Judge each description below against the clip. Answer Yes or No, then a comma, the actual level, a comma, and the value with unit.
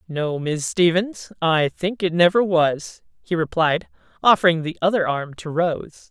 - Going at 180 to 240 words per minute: No, average, 155 wpm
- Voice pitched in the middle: Yes, medium, 170 Hz